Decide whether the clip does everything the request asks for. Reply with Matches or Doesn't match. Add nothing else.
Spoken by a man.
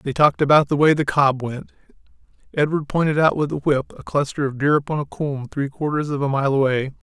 Matches